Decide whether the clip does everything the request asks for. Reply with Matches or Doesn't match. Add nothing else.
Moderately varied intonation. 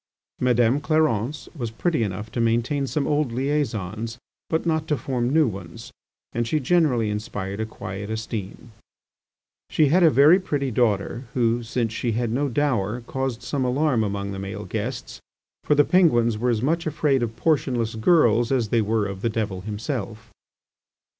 Matches